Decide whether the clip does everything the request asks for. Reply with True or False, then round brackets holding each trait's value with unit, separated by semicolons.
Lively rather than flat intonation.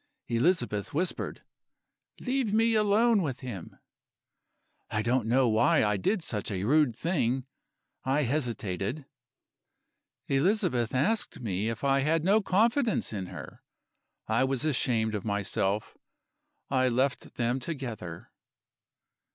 True (7.1 semitones)